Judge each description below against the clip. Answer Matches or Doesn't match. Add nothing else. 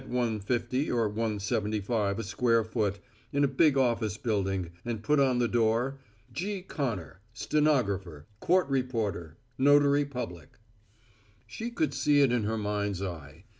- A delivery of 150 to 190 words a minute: Doesn't match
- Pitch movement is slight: Doesn't match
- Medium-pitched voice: Doesn't match